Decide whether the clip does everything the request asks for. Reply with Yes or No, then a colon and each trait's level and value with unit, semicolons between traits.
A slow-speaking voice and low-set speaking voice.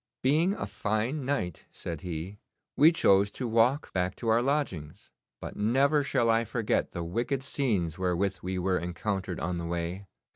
No: average, 170 wpm; low, 105 Hz